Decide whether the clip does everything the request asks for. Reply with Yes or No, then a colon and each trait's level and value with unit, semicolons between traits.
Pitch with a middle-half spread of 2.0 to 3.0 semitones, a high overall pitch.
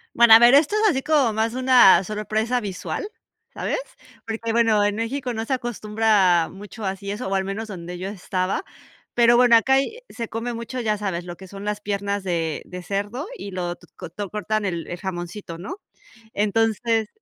No: average, 3.5 semitones; high, 210 Hz